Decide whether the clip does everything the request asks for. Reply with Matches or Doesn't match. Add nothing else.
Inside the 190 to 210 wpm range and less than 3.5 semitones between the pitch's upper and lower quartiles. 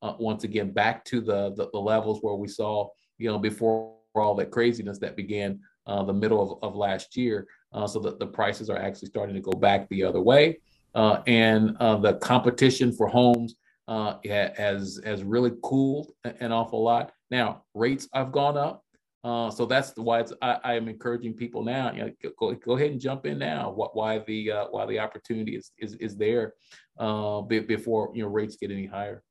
Matches